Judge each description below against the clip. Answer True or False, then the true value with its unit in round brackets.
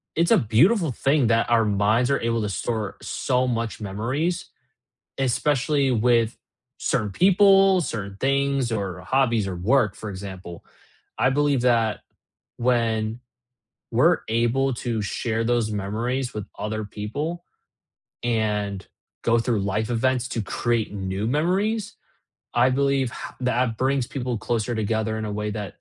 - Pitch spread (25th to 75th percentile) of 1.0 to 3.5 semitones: False (3.9 semitones)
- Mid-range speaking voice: False (115 Hz)